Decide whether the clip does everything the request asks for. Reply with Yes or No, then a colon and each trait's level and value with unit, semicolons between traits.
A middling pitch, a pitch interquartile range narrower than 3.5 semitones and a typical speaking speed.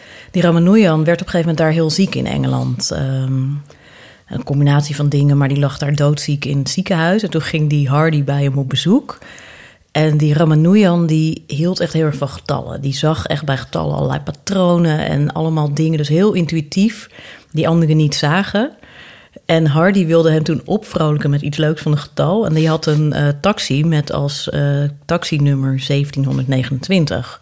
Yes: medium, 155 Hz; average, 2.8 semitones; average, 185 wpm